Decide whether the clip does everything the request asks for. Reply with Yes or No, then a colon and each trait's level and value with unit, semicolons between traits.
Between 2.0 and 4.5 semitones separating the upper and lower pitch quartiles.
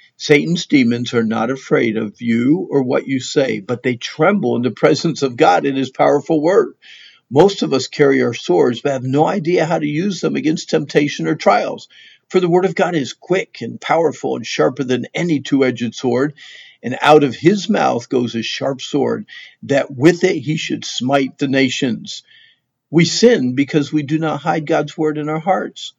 Yes: average, 4.1 semitones